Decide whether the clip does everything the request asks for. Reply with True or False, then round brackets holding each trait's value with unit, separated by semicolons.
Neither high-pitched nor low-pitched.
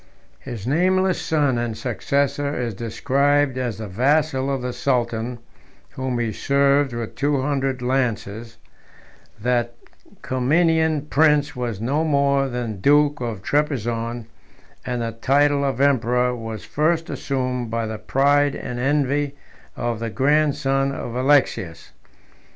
False (130 Hz)